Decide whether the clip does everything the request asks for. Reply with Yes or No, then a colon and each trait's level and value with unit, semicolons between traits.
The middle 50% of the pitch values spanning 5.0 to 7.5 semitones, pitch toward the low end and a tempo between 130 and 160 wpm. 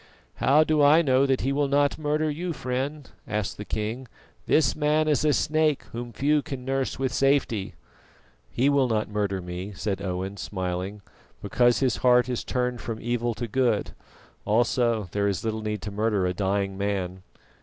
No: average, 5.3 semitones; low, 120 Hz; average, 175 wpm